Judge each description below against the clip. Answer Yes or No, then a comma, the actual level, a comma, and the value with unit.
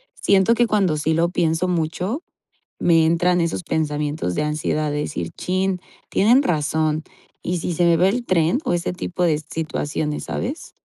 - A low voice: No, medium, 170 Hz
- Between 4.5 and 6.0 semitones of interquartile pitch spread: No, average, 2.9 semitones